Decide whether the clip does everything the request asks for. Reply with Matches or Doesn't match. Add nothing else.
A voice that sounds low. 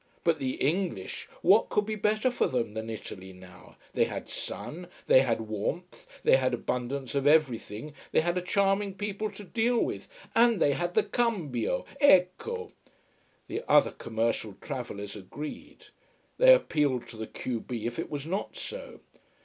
Doesn't match